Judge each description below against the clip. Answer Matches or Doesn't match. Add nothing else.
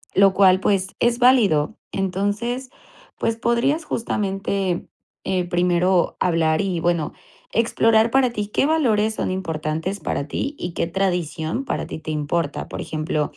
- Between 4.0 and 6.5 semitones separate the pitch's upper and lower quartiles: Matches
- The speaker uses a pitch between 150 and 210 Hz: Matches